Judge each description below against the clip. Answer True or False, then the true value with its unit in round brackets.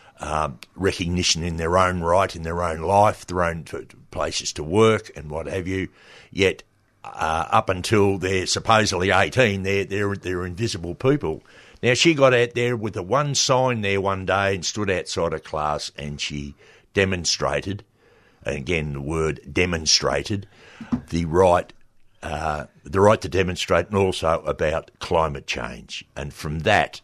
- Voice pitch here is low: True (95 Hz)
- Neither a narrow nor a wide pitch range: True (3.7 semitones)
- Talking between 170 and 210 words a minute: False (160 wpm)